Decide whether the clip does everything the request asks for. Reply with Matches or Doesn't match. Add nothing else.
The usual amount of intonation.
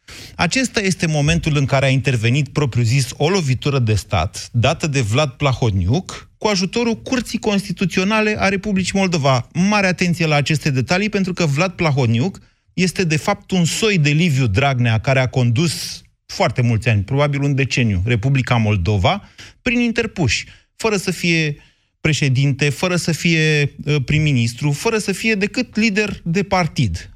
Doesn't match